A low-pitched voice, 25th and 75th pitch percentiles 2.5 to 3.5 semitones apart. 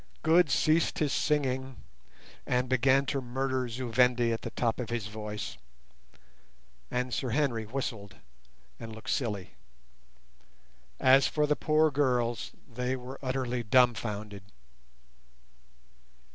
Yes: low, 125 Hz; average, 2.8 semitones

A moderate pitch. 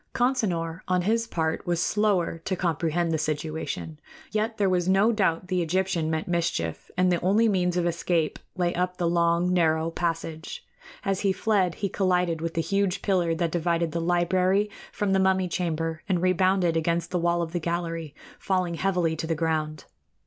Yes: medium, 175 Hz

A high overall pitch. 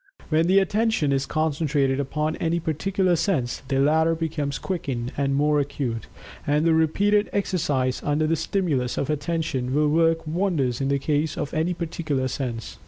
No: medium, 150 Hz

